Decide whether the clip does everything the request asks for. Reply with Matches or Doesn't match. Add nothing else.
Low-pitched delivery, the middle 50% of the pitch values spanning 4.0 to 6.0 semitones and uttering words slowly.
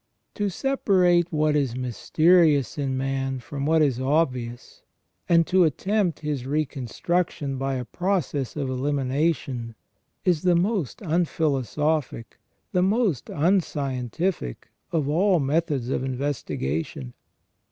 Doesn't match